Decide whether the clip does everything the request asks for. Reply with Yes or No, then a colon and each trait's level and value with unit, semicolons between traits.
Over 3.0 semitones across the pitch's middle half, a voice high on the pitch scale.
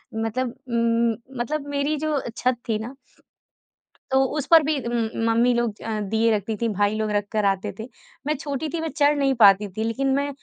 Yes: average, 4.3 semitones; high, 235 Hz